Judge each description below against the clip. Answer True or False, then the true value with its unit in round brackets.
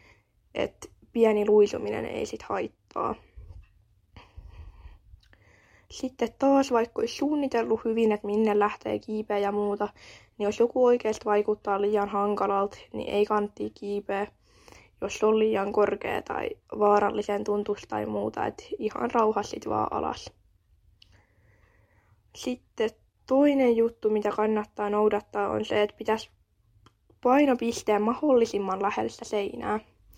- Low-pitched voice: False (205 Hz)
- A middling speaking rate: True (115 wpm)